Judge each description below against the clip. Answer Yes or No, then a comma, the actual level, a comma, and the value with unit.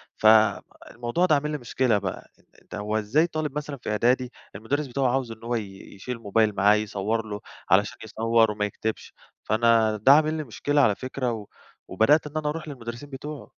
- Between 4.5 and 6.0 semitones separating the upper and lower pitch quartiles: Yes, average, 4.9 semitones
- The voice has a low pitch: Yes, low, 115 Hz